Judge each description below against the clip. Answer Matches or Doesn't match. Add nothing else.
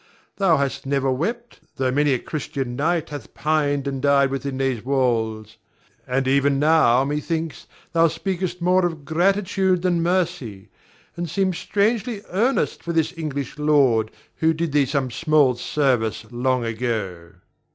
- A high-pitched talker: Doesn't match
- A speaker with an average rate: Matches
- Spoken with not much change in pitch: Doesn't match